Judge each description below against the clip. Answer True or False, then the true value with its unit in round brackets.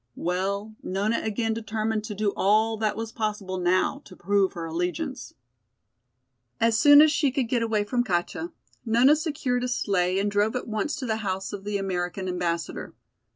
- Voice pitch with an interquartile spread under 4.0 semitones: True (3.6 semitones)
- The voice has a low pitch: False (215 Hz)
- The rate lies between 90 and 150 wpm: False (175 wpm)